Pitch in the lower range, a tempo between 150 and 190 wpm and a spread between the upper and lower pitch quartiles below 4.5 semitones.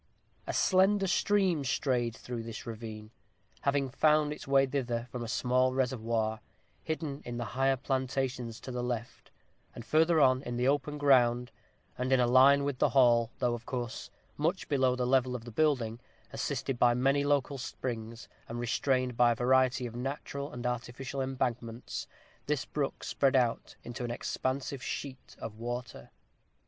Yes: low, 130 Hz; average, 165 wpm; narrow, 2.5 semitones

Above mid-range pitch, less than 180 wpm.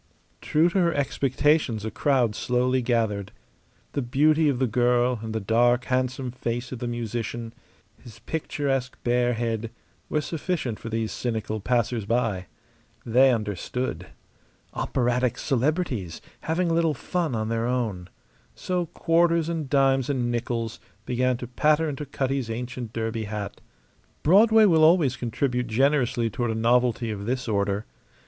No: low, 125 Hz; average, 145 wpm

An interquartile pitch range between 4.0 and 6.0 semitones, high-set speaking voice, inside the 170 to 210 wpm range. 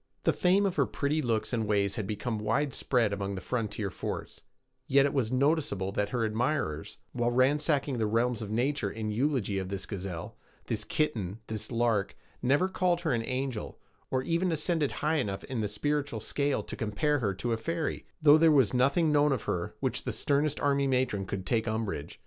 No: wide, 5.5 semitones; low, 125 Hz; average, 195 wpm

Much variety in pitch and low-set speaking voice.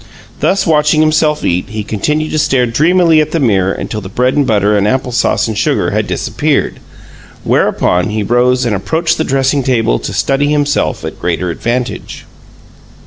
Yes: wide, 6.0 semitones; low, 125 Hz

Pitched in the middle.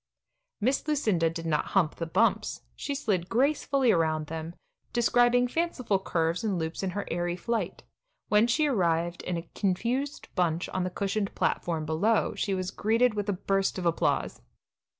No: high, 195 Hz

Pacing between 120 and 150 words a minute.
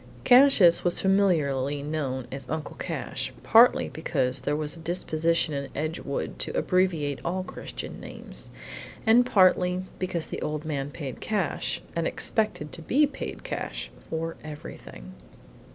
Yes: slow, 135 wpm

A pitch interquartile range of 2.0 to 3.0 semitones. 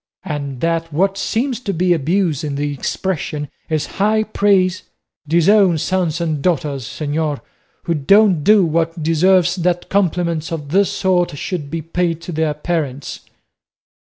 No: average, 3.6 semitones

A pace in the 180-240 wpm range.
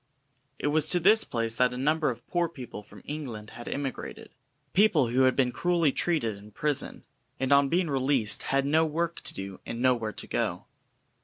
Yes: average, 190 wpm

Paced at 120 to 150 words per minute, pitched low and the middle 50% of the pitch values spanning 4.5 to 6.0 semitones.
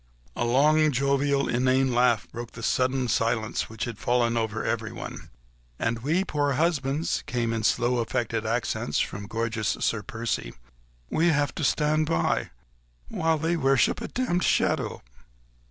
No: average, 145 wpm; low, 125 Hz; average, 4.1 semitones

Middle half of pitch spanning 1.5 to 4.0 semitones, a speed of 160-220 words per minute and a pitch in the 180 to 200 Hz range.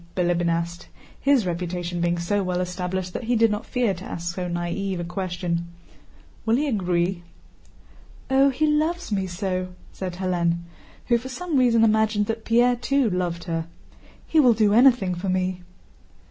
No: average, 5.0 semitones; average, 165 wpm; high, 190 Hz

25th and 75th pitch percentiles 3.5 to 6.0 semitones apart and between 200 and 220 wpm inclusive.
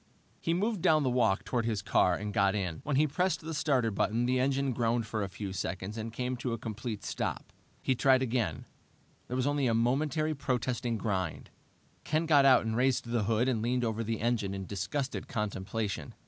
Yes: average, 4.0 semitones; fast, 205 wpm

